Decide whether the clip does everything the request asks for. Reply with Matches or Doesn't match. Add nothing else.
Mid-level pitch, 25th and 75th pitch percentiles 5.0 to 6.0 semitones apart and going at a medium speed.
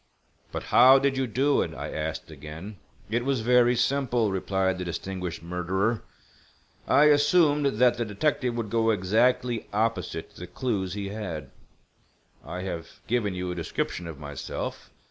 Doesn't match